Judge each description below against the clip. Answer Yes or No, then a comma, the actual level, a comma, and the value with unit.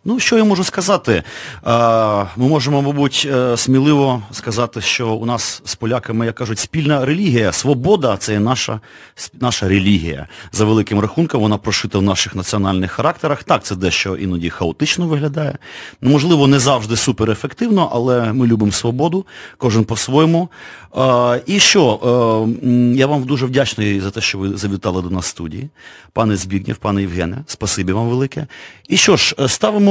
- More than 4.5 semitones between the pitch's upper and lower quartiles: Yes, average, 5.2 semitones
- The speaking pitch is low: Yes, low, 120 Hz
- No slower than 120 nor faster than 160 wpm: Yes, fast, 155 wpm